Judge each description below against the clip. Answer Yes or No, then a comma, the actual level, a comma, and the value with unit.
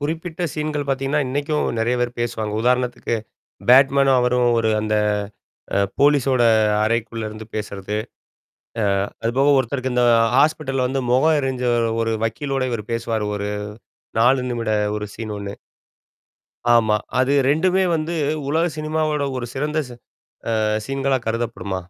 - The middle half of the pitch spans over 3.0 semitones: Yes, average, 3.9 semitones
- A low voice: Yes, low, 130 Hz